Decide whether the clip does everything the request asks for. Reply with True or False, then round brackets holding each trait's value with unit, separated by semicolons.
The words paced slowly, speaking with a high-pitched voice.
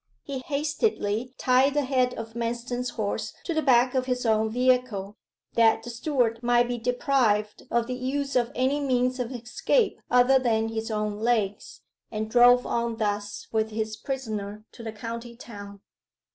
False (165 wpm; 240 Hz)